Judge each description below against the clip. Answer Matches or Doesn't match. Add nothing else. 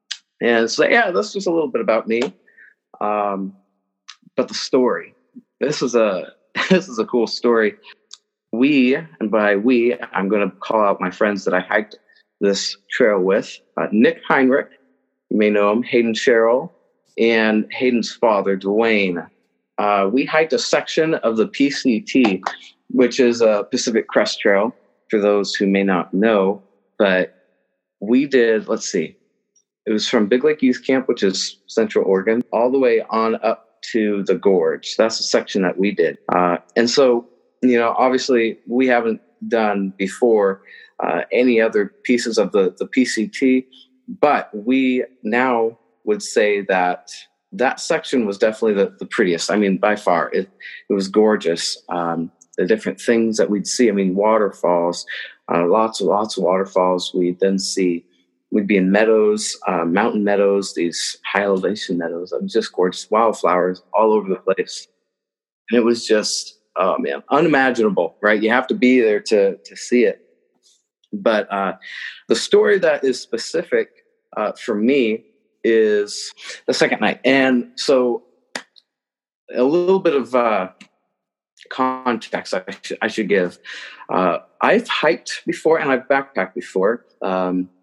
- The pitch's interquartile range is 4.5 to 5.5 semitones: Matches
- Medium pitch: Doesn't match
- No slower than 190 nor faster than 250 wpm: Doesn't match